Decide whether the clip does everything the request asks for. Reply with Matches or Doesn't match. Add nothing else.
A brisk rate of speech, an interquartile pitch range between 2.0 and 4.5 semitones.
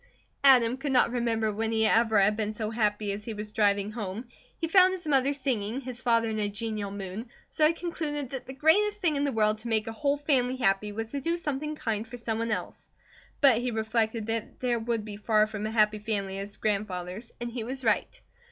Matches